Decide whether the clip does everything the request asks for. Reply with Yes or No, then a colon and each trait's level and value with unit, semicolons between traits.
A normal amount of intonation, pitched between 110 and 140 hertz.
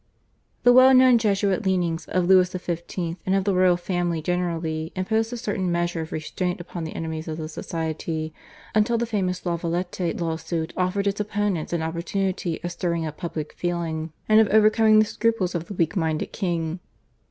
No: average, 3.3 semitones; medium, 175 Hz